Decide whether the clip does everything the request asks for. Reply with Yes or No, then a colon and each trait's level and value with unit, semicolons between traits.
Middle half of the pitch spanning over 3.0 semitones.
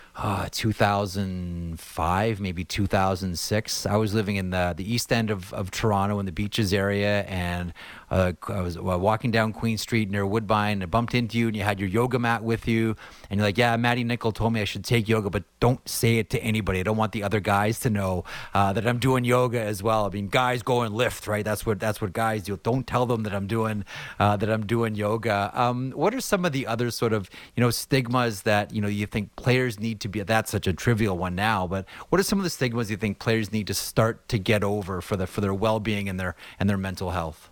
No: narrow, 2.6 semitones